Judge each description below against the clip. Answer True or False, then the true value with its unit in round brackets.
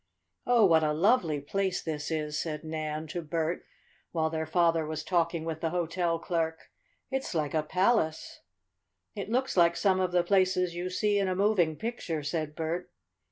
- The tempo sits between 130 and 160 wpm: False (175 wpm)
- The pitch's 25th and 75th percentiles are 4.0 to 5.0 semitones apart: False (2.8 semitones)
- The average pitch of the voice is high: False (170 Hz)